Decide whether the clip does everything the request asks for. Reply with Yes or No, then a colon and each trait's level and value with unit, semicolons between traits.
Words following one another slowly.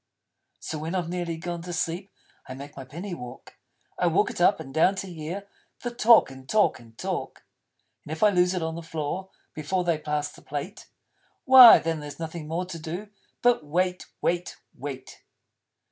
No: average, 190 wpm